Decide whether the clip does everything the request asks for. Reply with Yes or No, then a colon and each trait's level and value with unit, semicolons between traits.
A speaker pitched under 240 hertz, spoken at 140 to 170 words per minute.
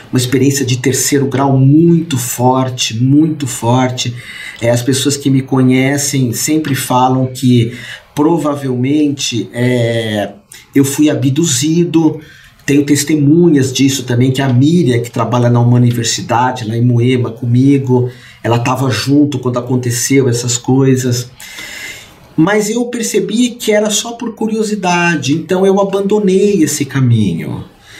No: low, 135 Hz; average, 125 wpm